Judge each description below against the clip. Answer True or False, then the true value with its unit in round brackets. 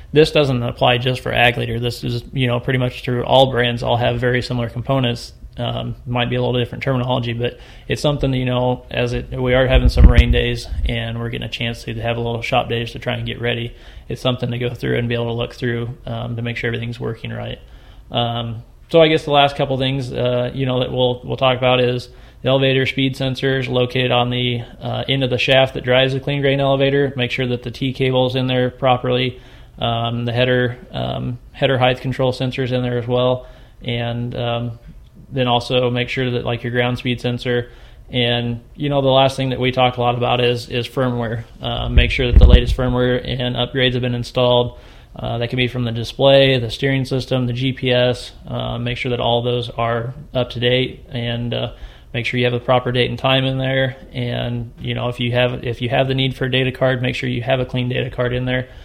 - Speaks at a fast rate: True (235 wpm)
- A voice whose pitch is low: True (125 Hz)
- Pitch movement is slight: True (1.3 semitones)